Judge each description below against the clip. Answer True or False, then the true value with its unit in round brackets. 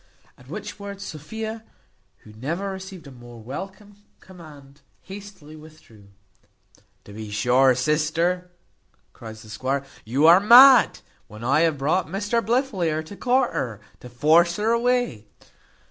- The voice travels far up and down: True (7.5 semitones)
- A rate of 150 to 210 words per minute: False (140 wpm)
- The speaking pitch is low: False (160 Hz)